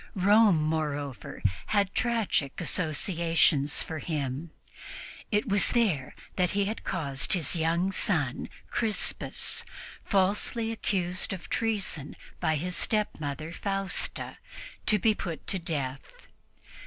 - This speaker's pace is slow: Yes, slow, 110 wpm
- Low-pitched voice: No, medium, 175 Hz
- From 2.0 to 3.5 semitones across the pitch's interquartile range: No, average, 4.9 semitones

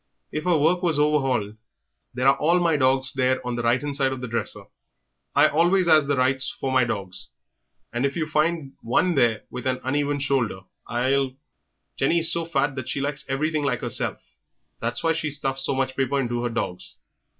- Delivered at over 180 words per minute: Yes, fast, 205 wpm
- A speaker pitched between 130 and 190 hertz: Yes, low, 135 Hz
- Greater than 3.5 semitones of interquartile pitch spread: No, average, 3.0 semitones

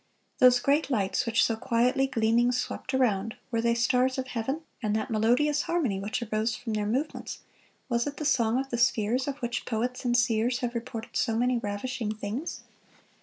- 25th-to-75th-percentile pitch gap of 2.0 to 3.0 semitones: Yes, narrow, 2.5 semitones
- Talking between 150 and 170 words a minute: No, average, 185 wpm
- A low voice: No, high, 240 Hz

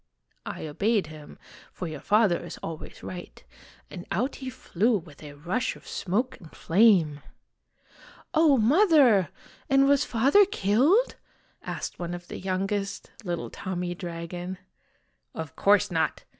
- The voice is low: No, high, 190 Hz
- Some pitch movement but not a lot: No, wide, 5.8 semitones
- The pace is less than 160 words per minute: Yes, average, 145 wpm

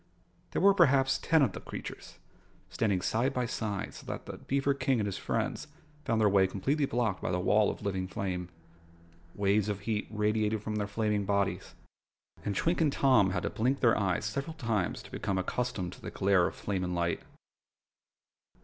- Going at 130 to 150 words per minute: No, average, 190 wpm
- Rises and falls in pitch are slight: No, average, 4.3 semitones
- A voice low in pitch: Yes, low, 105 Hz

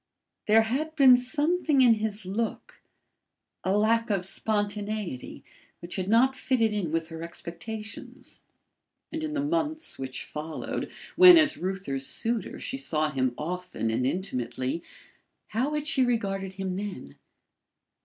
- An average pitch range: No, wide, 6.9 semitones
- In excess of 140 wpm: No, slow, 135 wpm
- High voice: Yes, high, 210 Hz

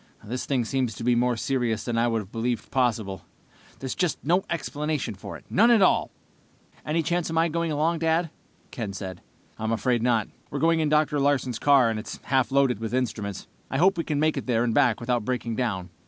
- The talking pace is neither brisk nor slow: No, fast, 215 wpm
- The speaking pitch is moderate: No, low, 130 Hz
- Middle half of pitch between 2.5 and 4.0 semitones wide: No, average, 5.0 semitones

